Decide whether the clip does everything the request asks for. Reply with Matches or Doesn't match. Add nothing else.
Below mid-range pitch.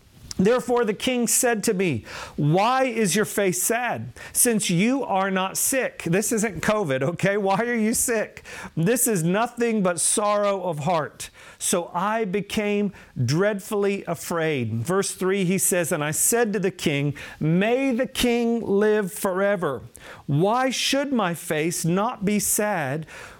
Doesn't match